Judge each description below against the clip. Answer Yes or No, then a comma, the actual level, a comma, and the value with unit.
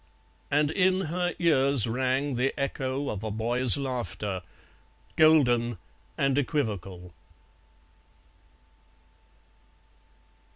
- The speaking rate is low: Yes, slow, 80 wpm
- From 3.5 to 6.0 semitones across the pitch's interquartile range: Yes, average, 3.9 semitones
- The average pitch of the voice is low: Yes, low, 130 Hz